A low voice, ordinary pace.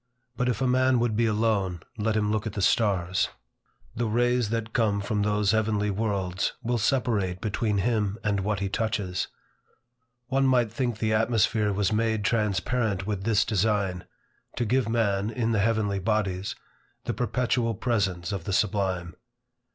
Yes: low, 105 Hz; average, 160 wpm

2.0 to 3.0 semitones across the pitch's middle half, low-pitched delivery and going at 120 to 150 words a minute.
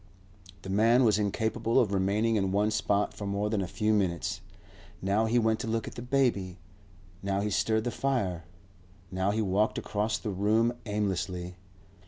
No: narrow, 2.4 semitones; low, 105 Hz; average, 175 wpm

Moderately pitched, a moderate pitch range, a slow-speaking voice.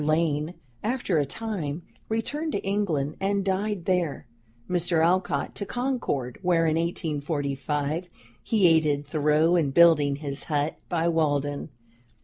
Yes: medium, 165 Hz; average, 4.3 semitones; slow, 125 wpm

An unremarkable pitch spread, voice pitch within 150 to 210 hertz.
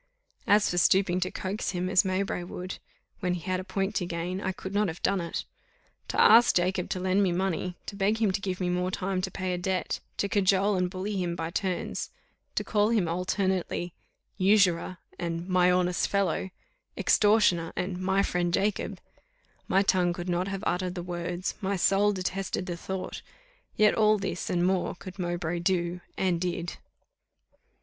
No: narrow, 1.7 semitones; medium, 185 Hz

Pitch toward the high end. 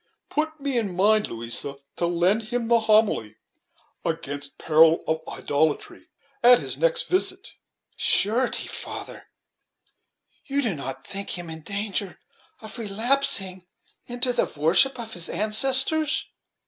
Yes: high, 210 Hz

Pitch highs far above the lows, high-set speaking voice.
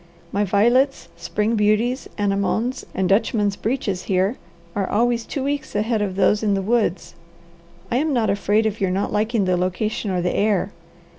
No: average, 2.9 semitones; high, 210 Hz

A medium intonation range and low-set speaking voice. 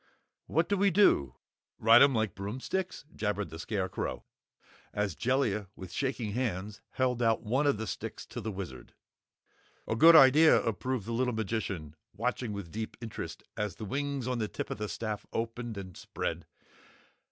Yes: average, 4.0 semitones; low, 115 Hz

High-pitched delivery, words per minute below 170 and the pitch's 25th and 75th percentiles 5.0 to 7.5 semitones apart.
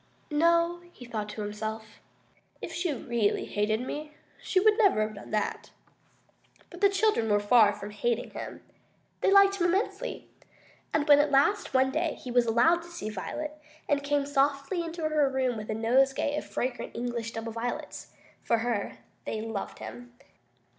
No: very high, 255 Hz; average, 175 wpm; wide, 5.6 semitones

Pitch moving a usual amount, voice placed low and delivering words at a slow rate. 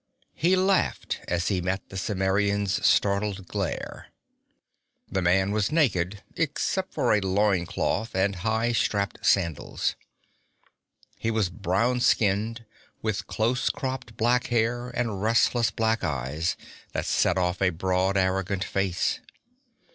Yes: average, 3.4 semitones; low, 100 Hz; slow, 125 wpm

